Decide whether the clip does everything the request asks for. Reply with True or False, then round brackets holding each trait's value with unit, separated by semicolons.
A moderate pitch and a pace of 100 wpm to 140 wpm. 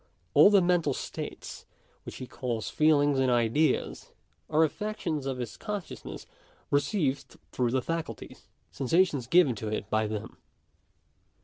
True (145 Hz; 135 wpm)